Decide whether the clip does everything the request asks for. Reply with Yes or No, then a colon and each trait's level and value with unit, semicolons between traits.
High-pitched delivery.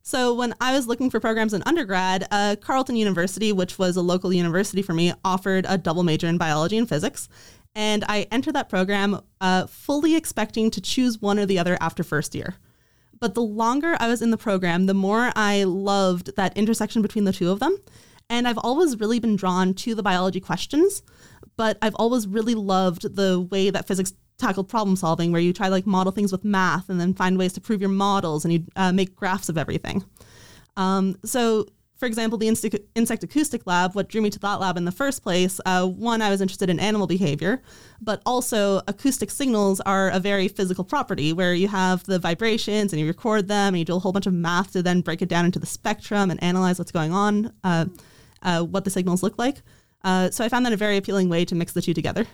Yes: high, 195 Hz